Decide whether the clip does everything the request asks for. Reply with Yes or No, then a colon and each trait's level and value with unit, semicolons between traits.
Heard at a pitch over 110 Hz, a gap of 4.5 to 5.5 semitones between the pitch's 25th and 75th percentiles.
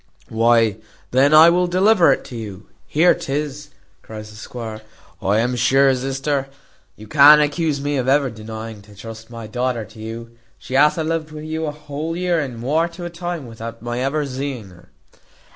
Yes: low, 135 Hz; average, 5.0 semitones